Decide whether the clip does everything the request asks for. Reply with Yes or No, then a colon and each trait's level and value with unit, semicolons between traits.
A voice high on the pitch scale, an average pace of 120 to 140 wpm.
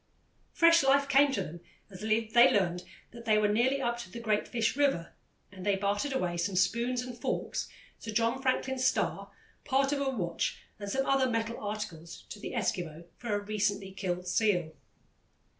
No: high, 220 Hz; average, 180 wpm